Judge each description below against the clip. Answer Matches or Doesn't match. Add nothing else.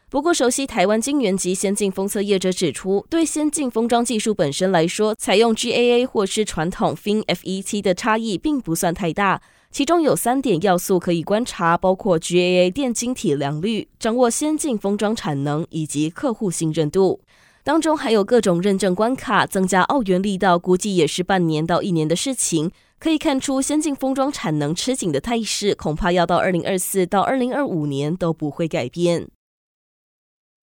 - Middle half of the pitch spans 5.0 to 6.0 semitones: Matches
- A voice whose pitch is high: Matches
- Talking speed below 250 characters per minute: Doesn't match